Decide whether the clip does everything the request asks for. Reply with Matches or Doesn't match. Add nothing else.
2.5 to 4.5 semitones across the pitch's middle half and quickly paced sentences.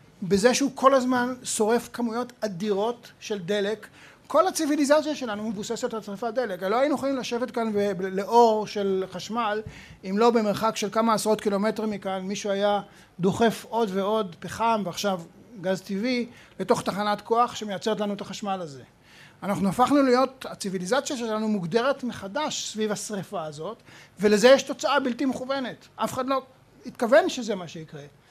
Matches